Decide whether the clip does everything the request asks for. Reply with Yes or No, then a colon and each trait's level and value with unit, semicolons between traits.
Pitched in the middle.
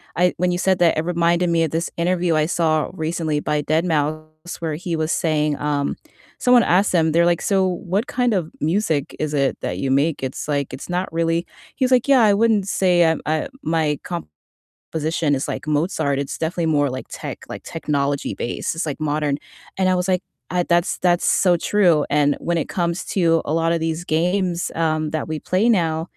Yes: medium, 165 Hz